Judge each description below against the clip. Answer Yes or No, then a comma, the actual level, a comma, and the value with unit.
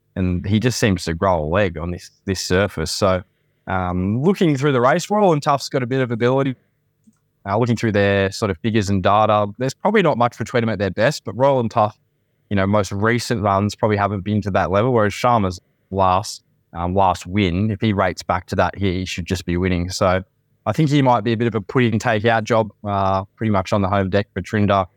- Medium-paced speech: No, fast, 245 wpm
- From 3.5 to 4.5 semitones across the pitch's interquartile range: Yes, average, 3.8 semitones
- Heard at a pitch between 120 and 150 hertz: No, low, 105 Hz